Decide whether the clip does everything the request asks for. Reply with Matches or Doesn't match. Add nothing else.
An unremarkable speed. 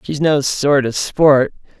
Matches